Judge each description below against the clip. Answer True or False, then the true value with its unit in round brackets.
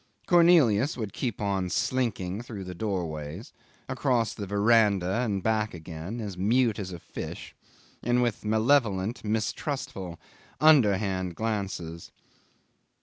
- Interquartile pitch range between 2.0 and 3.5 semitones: False (4.3 semitones)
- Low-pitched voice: True (105 Hz)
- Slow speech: True (115 wpm)